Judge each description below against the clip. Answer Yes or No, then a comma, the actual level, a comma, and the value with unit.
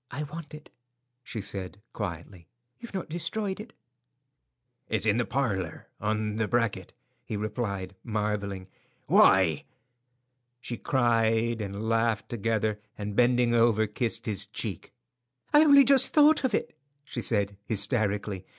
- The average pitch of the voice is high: No, low, 110 Hz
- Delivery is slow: Yes, slow, 130 wpm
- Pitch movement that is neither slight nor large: Yes, average, 3.4 semitones